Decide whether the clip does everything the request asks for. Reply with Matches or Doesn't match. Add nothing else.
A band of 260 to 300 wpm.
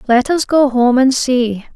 Doesn't match